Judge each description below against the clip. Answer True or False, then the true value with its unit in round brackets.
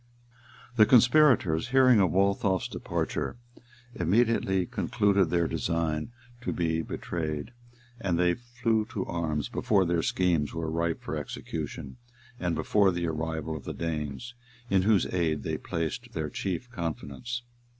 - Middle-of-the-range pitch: False (90 Hz)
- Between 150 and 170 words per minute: False (140 wpm)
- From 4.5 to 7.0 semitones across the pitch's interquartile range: True (5.1 semitones)